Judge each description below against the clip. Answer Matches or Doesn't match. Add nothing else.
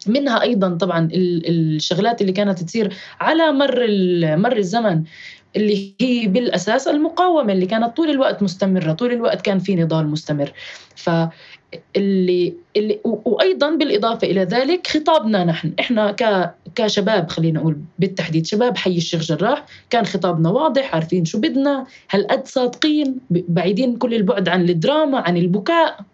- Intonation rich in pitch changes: Matches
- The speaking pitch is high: Matches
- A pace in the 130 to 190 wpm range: Matches